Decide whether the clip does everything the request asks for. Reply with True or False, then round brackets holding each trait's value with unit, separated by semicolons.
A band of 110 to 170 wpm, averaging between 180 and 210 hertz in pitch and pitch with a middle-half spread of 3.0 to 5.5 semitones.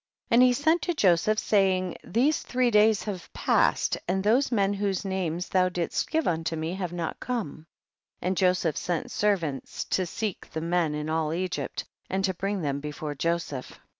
False (180 wpm; 185 Hz; 4.1 semitones)